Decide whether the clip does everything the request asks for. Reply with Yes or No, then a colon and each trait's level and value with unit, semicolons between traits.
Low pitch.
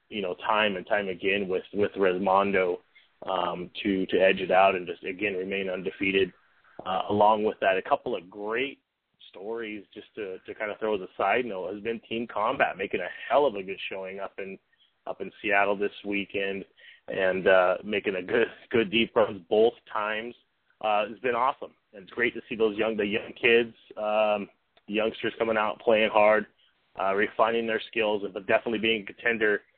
Yes: low, 105 Hz